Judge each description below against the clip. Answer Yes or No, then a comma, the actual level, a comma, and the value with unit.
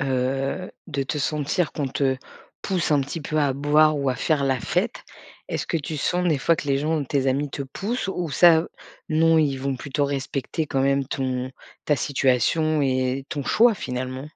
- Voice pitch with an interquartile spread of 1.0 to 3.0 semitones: Yes, narrow, 2.6 semitones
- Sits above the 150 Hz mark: No, medium, 140 Hz